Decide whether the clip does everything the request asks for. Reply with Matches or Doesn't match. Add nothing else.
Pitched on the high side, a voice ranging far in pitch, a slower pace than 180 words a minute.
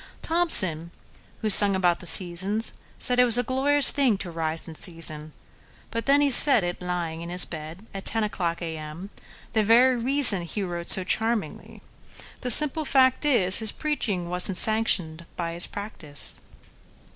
Matches